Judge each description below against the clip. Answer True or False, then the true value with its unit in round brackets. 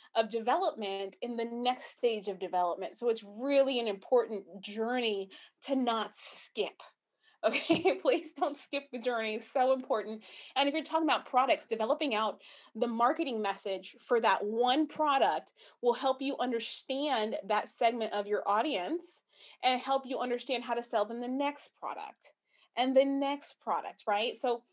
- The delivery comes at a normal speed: True (165 wpm)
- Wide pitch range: False (4.1 semitones)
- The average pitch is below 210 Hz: False (245 Hz)